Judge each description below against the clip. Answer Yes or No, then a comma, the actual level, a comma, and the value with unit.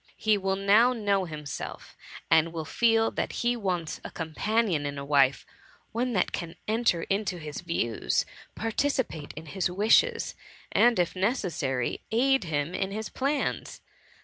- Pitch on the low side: No, high, 190 Hz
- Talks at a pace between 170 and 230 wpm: No, average, 145 wpm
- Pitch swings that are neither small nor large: No, wide, 5.9 semitones